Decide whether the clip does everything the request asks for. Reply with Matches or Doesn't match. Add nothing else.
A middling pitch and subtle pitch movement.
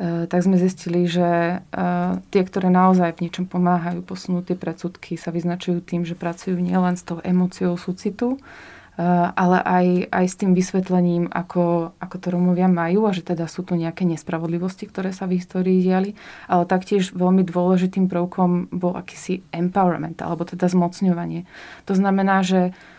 Matches